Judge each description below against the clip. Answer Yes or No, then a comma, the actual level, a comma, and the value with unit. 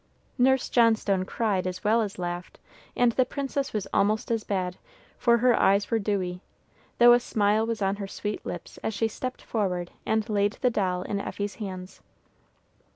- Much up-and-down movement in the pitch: No, average, 3.2 semitones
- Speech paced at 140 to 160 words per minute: No, average, 175 wpm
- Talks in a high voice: Yes, high, 210 Hz